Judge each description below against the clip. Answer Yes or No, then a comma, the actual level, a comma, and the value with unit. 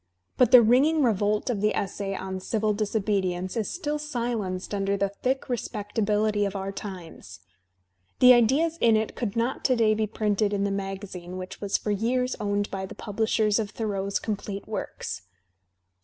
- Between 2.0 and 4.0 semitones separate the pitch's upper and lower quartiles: Yes, average, 2.8 semitones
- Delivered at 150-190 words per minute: Yes, average, 170 wpm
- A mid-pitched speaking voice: No, high, 210 Hz